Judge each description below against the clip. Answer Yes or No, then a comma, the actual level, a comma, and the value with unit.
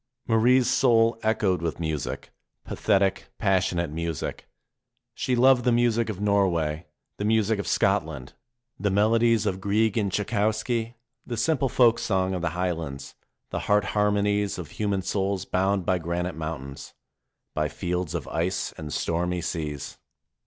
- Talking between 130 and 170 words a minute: Yes, average, 140 wpm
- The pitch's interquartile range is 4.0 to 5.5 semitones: Yes, average, 4.5 semitones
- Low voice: Yes, very low, 95 Hz